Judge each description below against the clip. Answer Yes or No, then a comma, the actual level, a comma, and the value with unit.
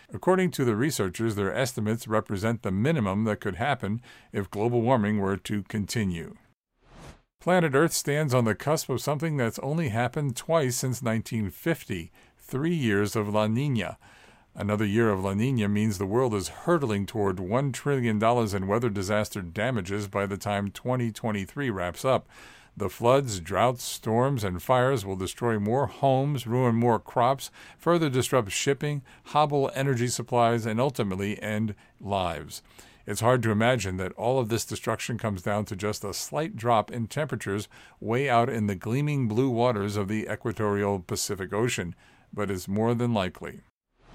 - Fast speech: No, average, 160 wpm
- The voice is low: Yes, low, 115 Hz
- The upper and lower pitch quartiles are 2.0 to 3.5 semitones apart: No, average, 3.9 semitones